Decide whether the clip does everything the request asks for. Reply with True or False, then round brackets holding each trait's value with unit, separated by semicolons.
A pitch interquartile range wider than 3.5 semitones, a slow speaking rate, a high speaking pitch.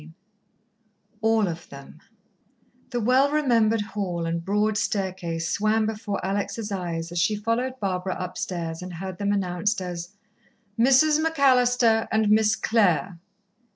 True (4.1 semitones; 130 wpm; 205 Hz)